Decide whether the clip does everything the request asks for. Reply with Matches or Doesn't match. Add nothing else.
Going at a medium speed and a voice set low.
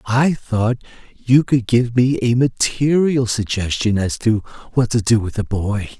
Matches